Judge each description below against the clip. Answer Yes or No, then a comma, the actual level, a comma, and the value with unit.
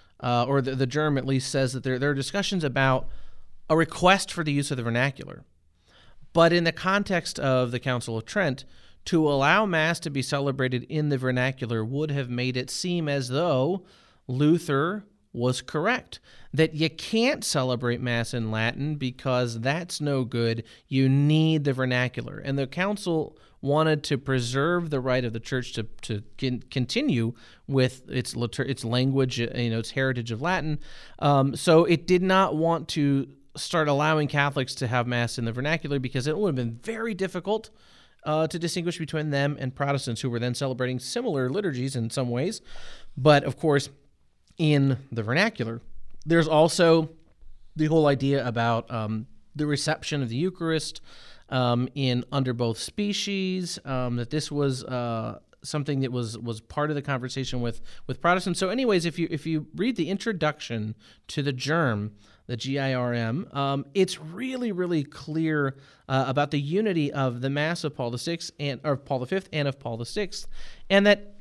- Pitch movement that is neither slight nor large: Yes, average, 4.3 semitones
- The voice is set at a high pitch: No, medium, 140 Hz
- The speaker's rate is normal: Yes, average, 180 wpm